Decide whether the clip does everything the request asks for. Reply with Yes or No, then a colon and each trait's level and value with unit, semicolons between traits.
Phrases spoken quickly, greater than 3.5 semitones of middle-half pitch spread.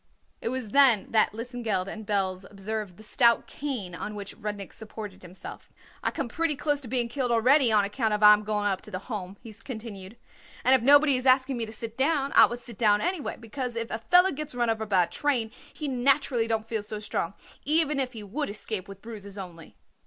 Yes: fast, 220 wpm; average, 4.0 semitones